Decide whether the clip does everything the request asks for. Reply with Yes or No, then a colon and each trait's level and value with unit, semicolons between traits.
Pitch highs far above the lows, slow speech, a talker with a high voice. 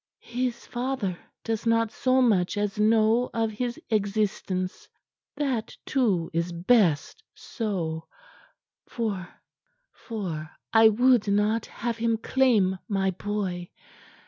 No: average, 3.6 semitones; slow, 105 wpm; high, 215 Hz